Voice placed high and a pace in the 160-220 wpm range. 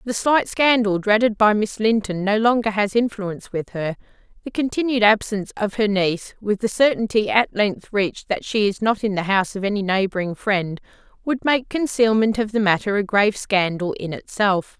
Yes: high, 210 Hz; average, 190 wpm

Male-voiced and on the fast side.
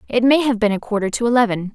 No: female; fast, 275 wpm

